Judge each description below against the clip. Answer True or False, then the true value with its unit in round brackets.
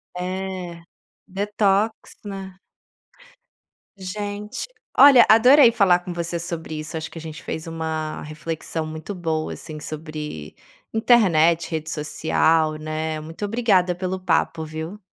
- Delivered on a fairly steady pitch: False (3.7 semitones)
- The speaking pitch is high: False (170 Hz)